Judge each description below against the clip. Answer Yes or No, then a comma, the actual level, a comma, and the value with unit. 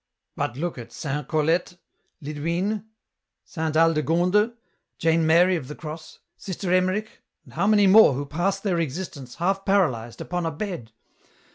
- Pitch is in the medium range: Yes, medium, 170 Hz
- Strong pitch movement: No, average, 3.8 semitones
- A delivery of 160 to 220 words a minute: No, average, 145 wpm